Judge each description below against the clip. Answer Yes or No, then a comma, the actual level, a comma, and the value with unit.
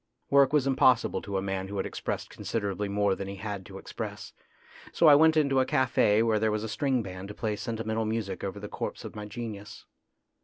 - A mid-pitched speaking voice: No, low, 110 Hz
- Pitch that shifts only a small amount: No, average, 3.4 semitones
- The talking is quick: Yes, fast, 225 wpm